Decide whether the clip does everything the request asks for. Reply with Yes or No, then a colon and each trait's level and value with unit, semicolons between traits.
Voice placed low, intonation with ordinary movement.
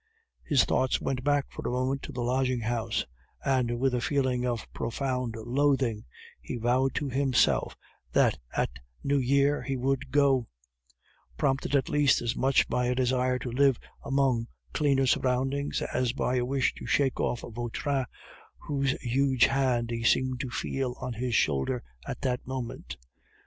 No: low, 130 Hz; narrow, 1.9 semitones